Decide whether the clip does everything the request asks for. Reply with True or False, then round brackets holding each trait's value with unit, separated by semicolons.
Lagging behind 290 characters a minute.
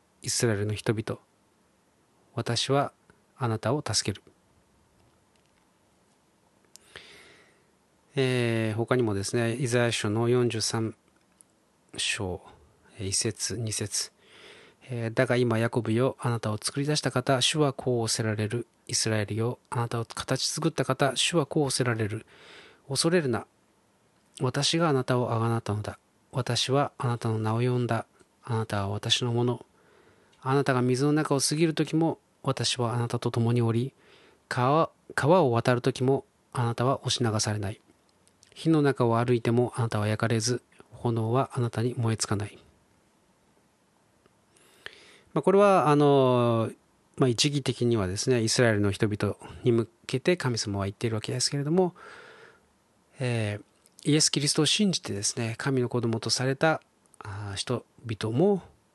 True (265 characters per minute)